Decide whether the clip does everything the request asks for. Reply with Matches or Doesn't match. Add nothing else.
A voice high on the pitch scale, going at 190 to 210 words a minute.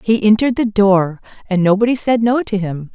Matches